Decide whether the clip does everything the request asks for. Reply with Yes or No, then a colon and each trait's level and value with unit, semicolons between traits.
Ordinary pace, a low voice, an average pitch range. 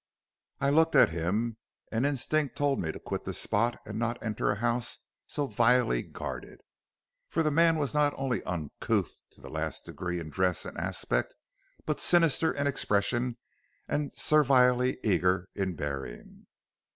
No: average, 155 wpm; low, 120 Hz; wide, 7.2 semitones